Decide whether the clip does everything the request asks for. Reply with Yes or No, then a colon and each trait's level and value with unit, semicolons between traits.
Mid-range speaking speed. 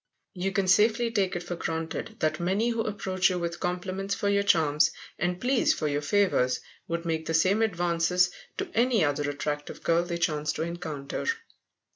Yes: average, 180 wpm